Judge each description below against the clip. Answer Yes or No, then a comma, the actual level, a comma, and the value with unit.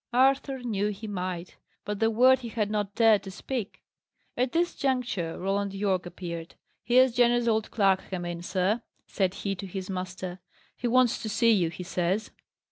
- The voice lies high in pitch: Yes, high, 205 Hz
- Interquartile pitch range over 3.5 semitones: Yes, average, 4.4 semitones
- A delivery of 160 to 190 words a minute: Yes, average, 180 wpm